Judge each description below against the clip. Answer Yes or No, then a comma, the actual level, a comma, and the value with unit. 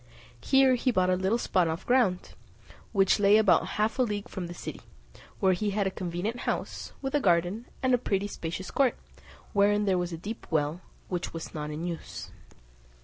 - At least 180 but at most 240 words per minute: Yes, average, 195 wpm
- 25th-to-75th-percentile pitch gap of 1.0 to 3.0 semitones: No, average, 3.9 semitones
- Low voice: No, high, 195 Hz